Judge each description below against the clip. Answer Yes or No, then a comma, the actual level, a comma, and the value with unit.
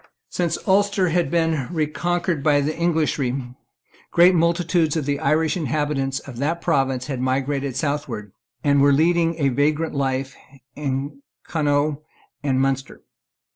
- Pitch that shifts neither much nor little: Yes, average, 3.3 semitones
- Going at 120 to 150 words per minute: Yes, slow, 135 wpm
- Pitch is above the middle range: No, medium, 145 Hz